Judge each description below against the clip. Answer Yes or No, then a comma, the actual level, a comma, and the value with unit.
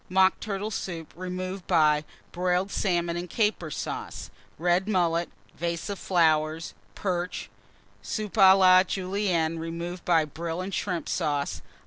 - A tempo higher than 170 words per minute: No, slow, 135 wpm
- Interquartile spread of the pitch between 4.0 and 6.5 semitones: No, narrow, 2.4 semitones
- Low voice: No, medium, 175 Hz